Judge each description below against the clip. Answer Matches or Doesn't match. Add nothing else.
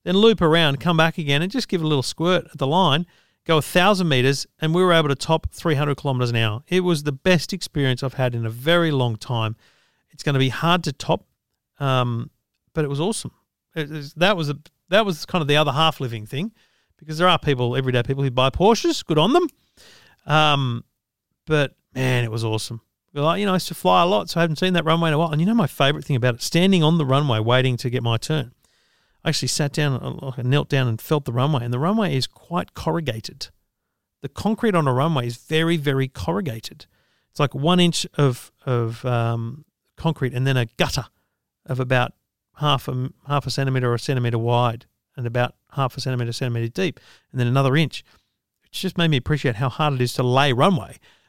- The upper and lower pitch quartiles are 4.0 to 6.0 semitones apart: Matches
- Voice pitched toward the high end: Doesn't match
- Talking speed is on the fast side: Matches